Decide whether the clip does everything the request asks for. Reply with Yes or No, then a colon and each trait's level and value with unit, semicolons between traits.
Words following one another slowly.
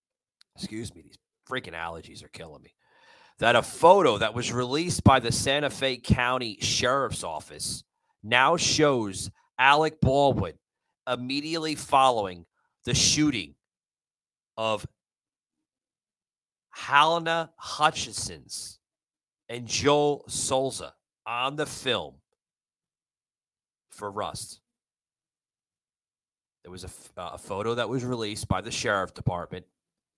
Yes: slow, 105 wpm